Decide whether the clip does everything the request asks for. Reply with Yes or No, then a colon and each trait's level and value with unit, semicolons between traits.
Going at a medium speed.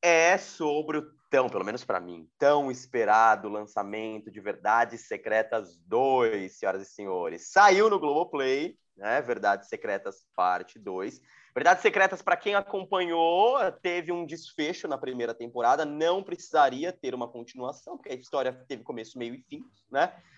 Yes: average, 150 wpm